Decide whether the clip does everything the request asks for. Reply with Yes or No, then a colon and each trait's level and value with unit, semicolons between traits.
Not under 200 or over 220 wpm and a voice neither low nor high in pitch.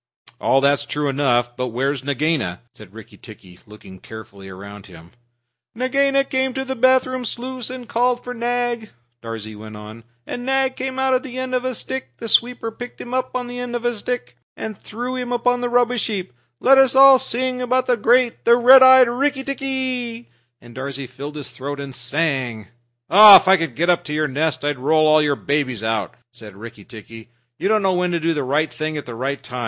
Yes: fast, 205 wpm; medium, 175 Hz